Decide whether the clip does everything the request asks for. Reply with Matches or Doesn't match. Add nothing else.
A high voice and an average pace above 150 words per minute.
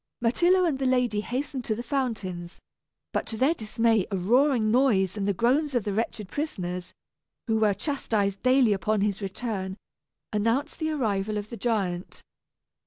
Matches